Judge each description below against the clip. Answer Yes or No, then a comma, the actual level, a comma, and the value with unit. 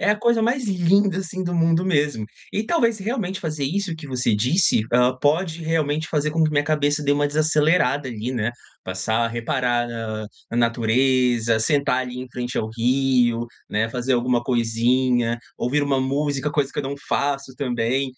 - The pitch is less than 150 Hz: Yes, low, 135 Hz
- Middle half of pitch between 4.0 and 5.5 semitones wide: Yes, average, 4.7 semitones